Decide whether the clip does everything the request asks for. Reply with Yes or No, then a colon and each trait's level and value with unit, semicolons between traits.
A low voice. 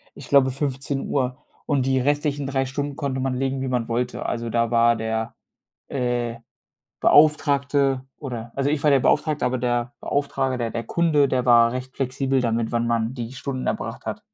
Yes: low, 130 Hz